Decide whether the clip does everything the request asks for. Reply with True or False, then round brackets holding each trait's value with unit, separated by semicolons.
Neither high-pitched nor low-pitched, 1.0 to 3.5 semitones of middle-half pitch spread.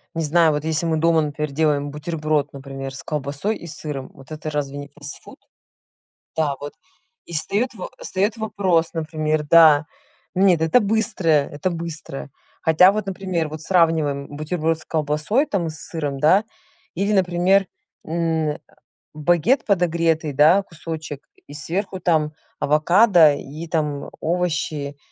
True (160 Hz; 2.9 semitones)